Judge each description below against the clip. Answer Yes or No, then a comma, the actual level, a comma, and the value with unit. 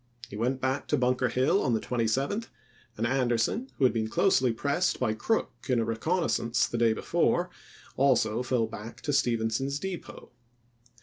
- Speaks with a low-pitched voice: Yes, low, 125 Hz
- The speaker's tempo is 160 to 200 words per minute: Yes, average, 175 wpm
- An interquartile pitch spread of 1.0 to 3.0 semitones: No, average, 3.4 semitones